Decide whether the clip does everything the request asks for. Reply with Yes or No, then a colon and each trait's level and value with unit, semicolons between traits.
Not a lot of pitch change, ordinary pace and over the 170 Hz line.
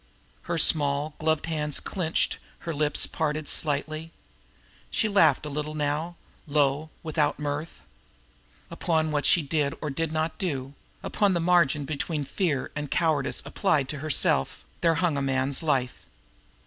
No: narrow, 2.2 semitones; average, 150 wpm; medium, 150 Hz